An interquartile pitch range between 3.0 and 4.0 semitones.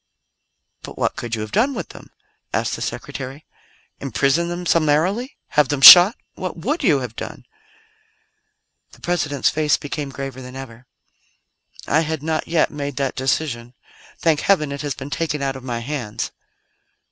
Yes: average, 3.5 semitones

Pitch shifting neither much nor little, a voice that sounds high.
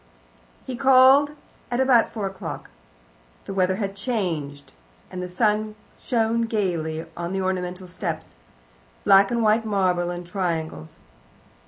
Yes: average, 4.2 semitones; high, 195 Hz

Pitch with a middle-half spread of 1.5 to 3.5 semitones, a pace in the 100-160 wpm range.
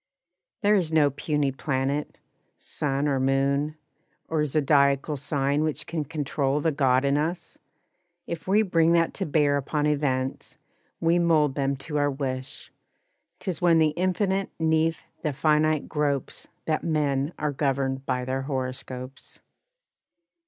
Yes: average, 2.7 semitones; average, 140 wpm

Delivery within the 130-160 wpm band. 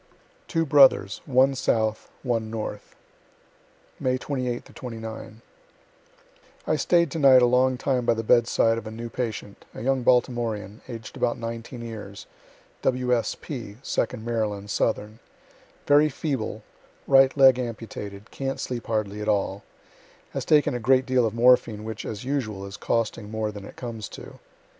Yes: average, 150 wpm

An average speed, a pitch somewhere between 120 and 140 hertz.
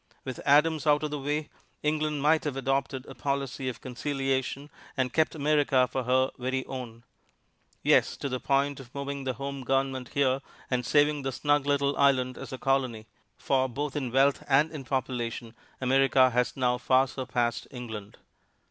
Yes: average, 170 wpm; low, 135 Hz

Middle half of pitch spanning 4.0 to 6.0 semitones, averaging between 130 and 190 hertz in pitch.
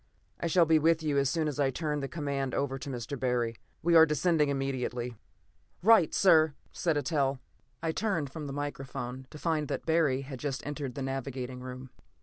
No: average, 3.2 semitones; medium, 140 Hz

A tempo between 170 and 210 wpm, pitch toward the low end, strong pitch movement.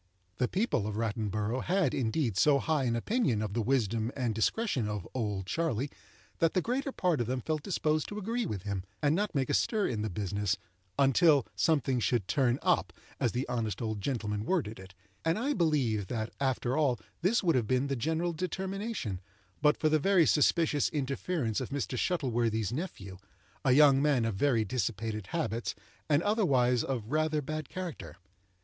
Yes: average, 180 wpm; low, 130 Hz; wide, 6.3 semitones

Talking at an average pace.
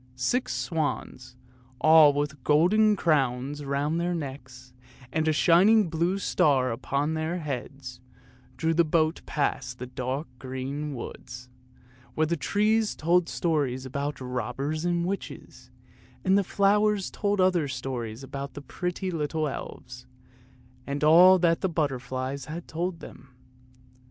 No: slow, 130 wpm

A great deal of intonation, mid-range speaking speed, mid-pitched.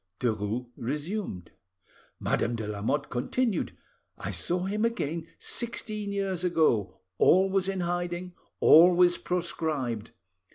No: wide, 7.3 semitones; slow, 100 wpm; medium, 175 Hz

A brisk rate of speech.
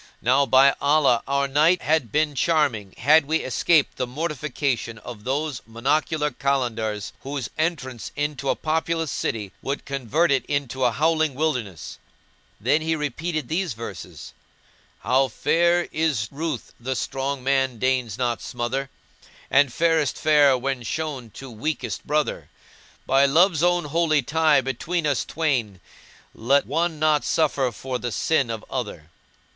No: average, 145 wpm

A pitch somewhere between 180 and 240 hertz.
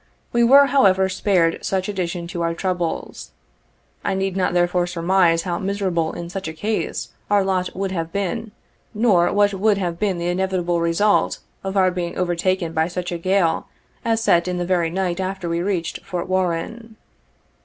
Yes: medium, 185 Hz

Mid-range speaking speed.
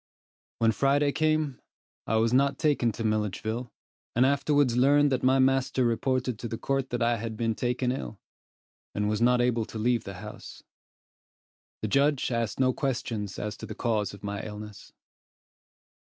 Yes: average, 165 wpm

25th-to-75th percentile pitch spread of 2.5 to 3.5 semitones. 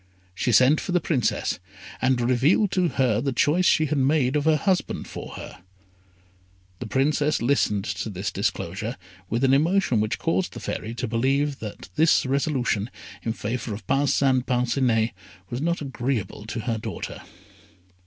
No: average, 4.4 semitones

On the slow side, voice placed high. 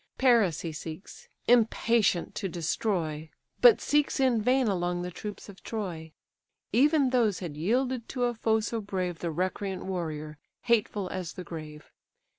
No: average, 150 wpm; high, 195 Hz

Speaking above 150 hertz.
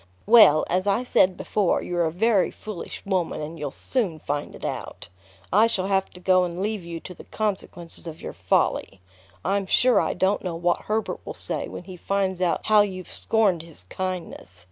Yes: medium, 185 Hz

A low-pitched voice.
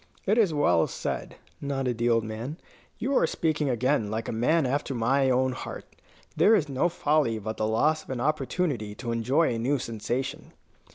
Yes: low, 130 Hz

